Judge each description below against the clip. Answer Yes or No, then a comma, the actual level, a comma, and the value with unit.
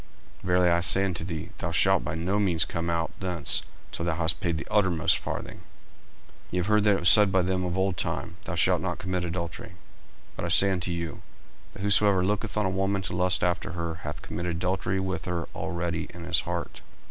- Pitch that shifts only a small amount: Yes, narrow, 2.0 semitones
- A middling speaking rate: No, fast, 225 wpm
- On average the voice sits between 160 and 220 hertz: No, very low, 90 Hz